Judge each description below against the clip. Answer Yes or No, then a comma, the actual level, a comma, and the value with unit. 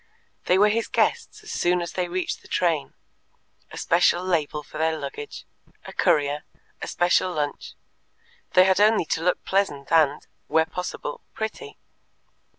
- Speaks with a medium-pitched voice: Yes, medium, 175 Hz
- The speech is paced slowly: No, average, 155 wpm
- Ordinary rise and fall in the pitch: Yes, average, 3.4 semitones